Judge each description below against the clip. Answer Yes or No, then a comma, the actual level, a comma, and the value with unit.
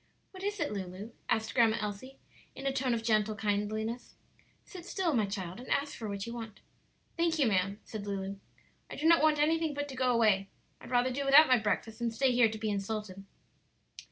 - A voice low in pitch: No, high, 230 Hz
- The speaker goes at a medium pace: No, fast, 210 wpm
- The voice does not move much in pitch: No, average, 4.8 semitones